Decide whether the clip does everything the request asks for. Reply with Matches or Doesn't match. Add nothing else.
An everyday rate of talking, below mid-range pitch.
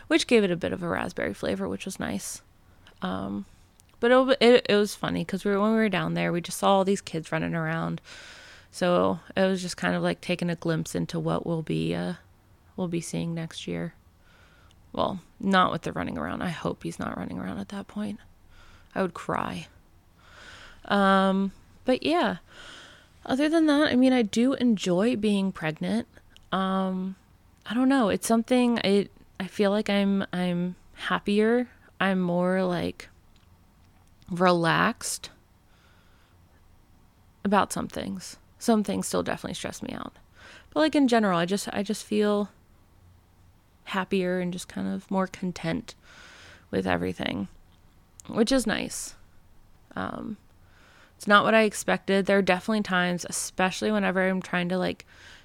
Doesn't match